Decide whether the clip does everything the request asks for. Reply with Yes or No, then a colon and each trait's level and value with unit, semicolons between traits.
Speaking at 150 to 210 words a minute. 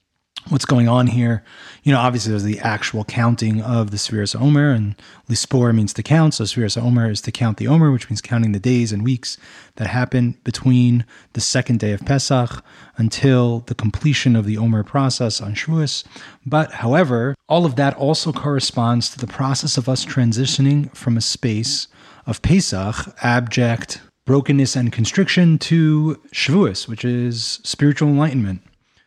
Yes: average, 165 wpm